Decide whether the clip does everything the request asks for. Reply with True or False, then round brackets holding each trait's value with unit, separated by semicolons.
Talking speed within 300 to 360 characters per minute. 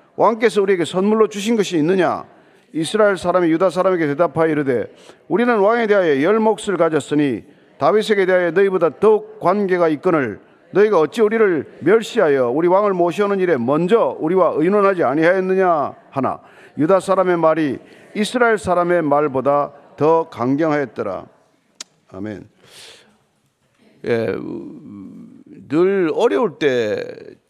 True (310 characters per minute)